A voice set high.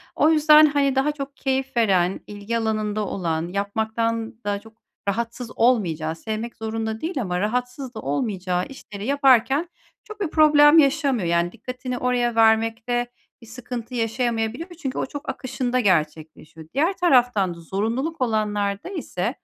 Yes: high, 230 Hz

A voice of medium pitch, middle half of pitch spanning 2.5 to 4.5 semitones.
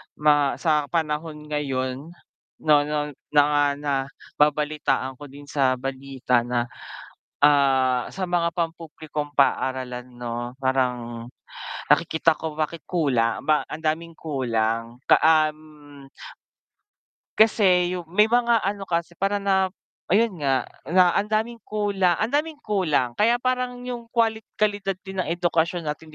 No: medium, 155 Hz; wide, 5.4 semitones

